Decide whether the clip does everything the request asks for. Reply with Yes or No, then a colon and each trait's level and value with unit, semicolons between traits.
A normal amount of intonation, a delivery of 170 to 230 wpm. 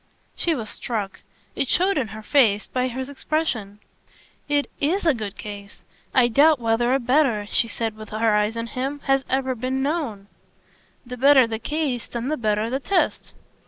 Yes: average, 4.4 semitones; average, 180 wpm